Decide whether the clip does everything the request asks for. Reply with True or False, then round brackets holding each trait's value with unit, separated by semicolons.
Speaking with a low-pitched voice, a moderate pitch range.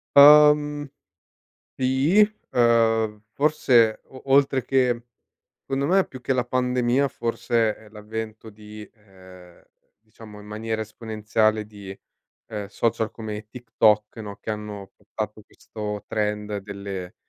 True (110 Hz; 3.1 semitones)